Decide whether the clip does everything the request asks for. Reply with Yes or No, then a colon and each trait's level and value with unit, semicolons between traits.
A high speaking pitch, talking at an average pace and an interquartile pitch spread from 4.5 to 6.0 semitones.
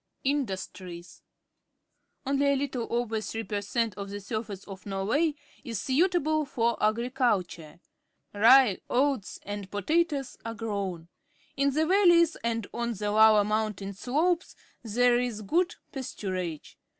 No: high, 230 Hz; slow, 130 wpm; average, 5.3 semitones